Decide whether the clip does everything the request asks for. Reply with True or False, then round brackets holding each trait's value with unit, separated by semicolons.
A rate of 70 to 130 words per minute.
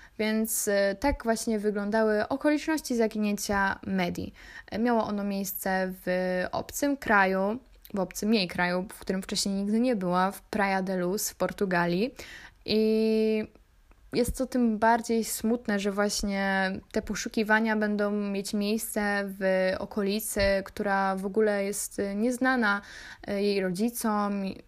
True (125 wpm)